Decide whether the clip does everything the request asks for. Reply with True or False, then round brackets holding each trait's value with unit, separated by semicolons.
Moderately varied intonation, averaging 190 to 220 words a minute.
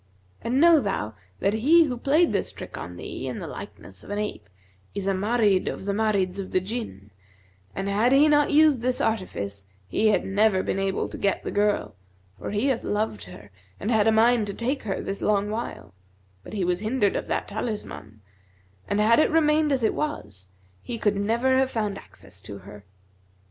True (4.1 semitones; 200 wpm)